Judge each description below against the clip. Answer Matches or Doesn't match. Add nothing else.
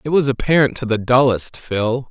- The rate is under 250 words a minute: Matches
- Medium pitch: Doesn't match